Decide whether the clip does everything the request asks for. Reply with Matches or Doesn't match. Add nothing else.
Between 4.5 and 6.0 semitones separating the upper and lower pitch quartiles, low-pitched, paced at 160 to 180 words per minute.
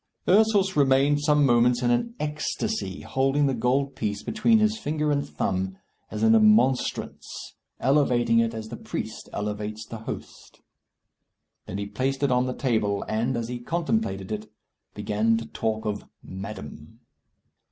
Doesn't match